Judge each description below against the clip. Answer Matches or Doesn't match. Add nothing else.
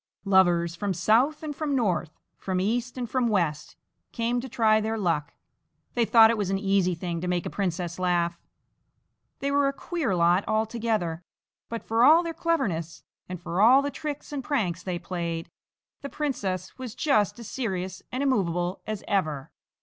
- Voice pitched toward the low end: Doesn't match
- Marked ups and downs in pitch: Matches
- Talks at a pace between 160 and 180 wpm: Matches